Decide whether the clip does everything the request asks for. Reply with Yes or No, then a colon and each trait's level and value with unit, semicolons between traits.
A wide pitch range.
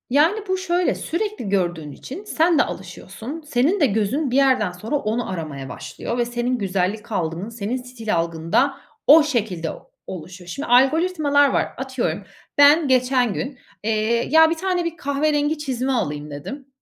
Yes: wide, 7.0 semitones